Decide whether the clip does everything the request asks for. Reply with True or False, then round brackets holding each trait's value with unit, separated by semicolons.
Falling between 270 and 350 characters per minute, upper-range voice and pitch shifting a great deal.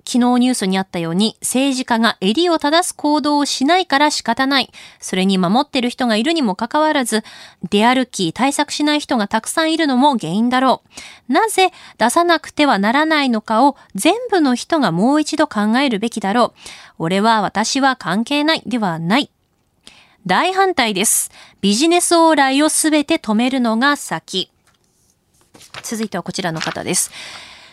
True (320 characters per minute; 255 Hz; 5.7 semitones)